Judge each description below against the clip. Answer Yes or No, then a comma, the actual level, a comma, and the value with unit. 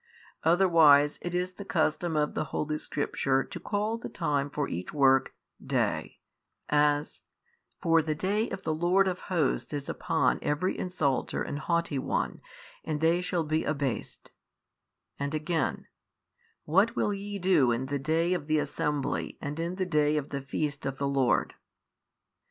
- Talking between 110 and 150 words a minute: No, average, 160 wpm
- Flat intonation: No, average, 3.7 semitones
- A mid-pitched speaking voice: Yes, medium, 155 Hz